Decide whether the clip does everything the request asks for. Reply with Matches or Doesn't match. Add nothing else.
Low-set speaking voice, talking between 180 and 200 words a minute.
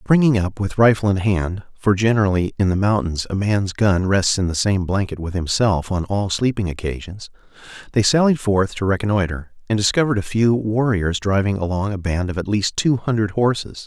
Matches